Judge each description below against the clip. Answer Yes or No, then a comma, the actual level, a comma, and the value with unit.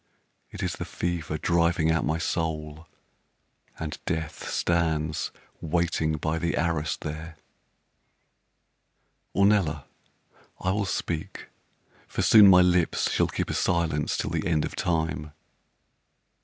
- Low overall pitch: Yes, very low, 80 Hz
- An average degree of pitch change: No, narrow, 1.7 semitones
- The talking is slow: Yes, slow, 120 wpm